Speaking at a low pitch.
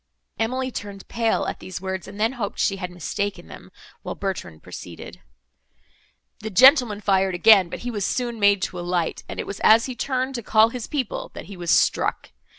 No: high, 205 Hz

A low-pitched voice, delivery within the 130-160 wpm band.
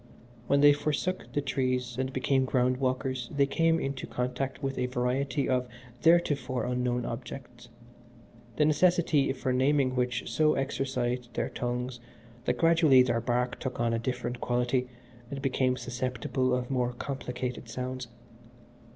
Yes: low, 130 Hz; average, 140 wpm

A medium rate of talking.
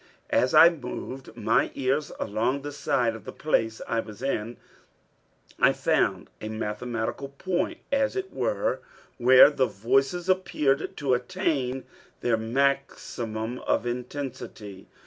No: slow, 125 wpm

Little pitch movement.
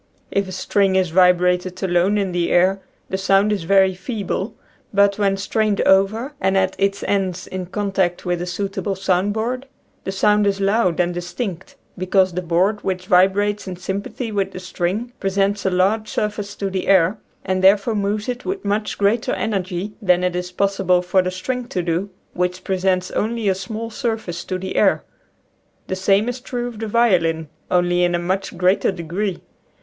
Yes: narrow, 2.3 semitones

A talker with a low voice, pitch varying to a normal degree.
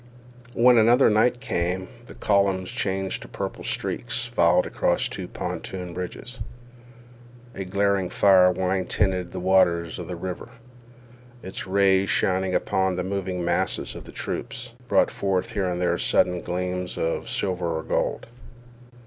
No: very low, 95 Hz; narrow, 1.6 semitones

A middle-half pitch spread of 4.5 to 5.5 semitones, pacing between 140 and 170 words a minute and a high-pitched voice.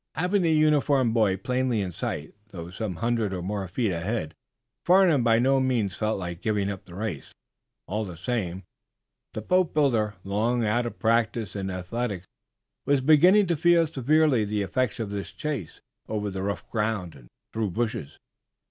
No: average, 5.1 semitones; average, 165 wpm; low, 110 Hz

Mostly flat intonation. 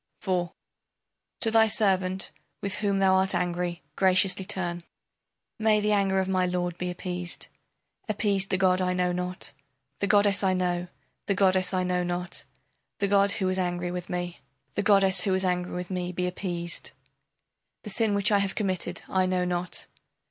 Yes: narrow, 1.7 semitones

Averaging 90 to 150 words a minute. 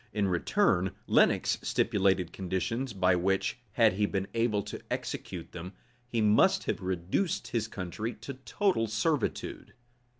Yes: slow, 135 wpm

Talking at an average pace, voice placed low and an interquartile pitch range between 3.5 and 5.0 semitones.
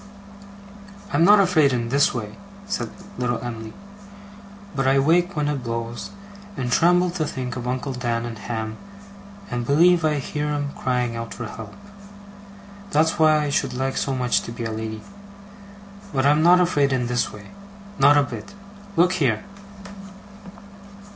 Yes: average, 160 wpm; low, 130 Hz; average, 4.5 semitones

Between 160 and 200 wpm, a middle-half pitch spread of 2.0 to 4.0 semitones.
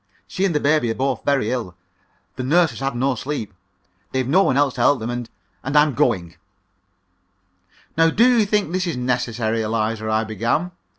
No: average, 190 wpm; average, 5.3 semitones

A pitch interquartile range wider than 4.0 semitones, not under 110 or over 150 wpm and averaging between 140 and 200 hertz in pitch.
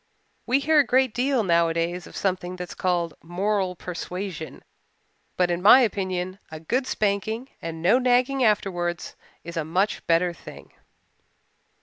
Yes: average, 4.7 semitones; average, 145 wpm; medium, 185 Hz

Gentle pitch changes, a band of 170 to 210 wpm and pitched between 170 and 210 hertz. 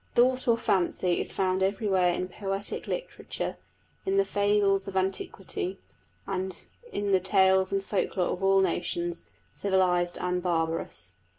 No: narrow, 1.8 semitones; average, 140 wpm; high, 190 Hz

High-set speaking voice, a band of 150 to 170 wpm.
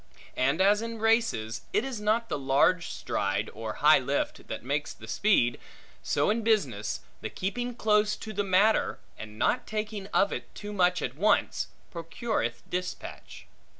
Yes: high, 195 Hz; average, 160 wpm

